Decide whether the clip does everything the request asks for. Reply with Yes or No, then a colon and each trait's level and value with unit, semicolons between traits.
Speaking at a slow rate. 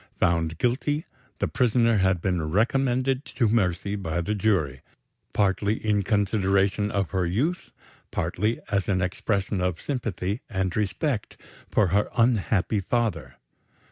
Yes: slow, 130 wpm